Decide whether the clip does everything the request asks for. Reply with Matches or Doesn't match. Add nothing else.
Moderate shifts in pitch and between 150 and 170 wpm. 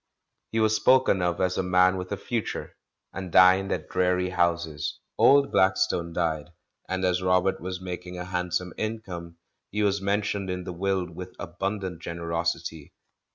Doesn't match